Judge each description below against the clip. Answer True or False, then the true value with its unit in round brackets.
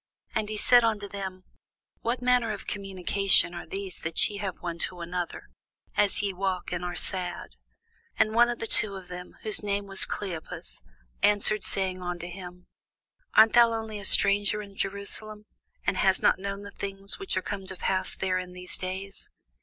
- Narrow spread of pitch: True (2.3 semitones)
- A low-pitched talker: False (195 Hz)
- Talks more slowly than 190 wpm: True (175 wpm)